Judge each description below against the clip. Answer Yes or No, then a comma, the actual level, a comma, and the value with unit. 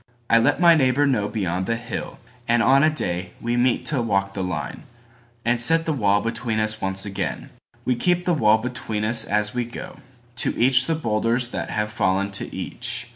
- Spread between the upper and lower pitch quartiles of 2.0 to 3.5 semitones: Yes, average, 3.2 semitones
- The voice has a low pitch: Yes, low, 115 Hz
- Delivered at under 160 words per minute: No, average, 180 wpm